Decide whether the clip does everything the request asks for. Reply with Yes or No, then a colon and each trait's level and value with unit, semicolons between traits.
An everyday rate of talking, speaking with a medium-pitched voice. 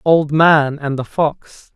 Yes: average, 170 wpm; medium, 150 Hz